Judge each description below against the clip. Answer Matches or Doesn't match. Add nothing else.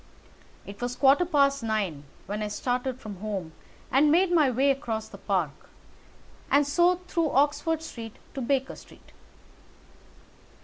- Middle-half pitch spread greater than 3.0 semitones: Matches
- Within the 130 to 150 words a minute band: Matches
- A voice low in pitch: Doesn't match